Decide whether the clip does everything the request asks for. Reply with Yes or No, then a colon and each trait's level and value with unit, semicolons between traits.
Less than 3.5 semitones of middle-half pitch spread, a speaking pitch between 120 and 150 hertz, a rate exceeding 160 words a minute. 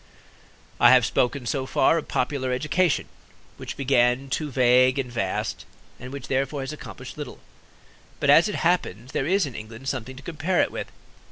Yes: average, 2.9 semitones; low, 135 Hz; average, 175 wpm